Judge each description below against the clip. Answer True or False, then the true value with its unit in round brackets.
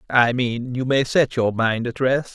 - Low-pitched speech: True (125 Hz)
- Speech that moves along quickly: True (230 wpm)